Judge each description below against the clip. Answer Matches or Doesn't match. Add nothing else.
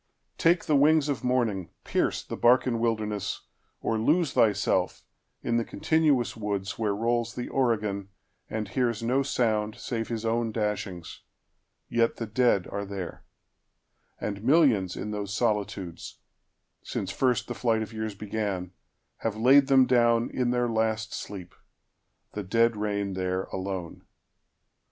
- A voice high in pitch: Doesn't match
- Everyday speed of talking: Doesn't match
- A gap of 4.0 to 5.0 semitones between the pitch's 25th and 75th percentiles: Doesn't match